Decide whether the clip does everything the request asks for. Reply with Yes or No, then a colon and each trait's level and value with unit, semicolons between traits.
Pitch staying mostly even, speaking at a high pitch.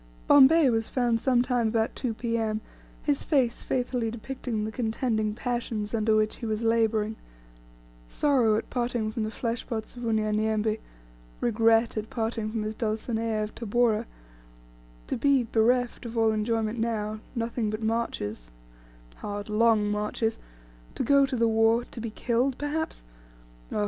Yes: narrow, 1.9 semitones; high, 225 Hz